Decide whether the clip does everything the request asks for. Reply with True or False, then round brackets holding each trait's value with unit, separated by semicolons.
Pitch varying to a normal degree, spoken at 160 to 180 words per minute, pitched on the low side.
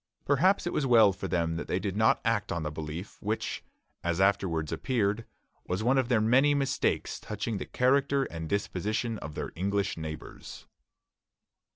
False (6.1 semitones; 170 wpm; 105 Hz)